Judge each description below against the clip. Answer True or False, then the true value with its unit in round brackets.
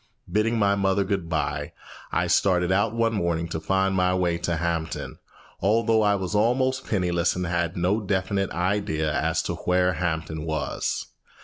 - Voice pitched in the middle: False (90 Hz)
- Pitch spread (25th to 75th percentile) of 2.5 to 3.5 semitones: True (3.1 semitones)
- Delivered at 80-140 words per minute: False (165 wpm)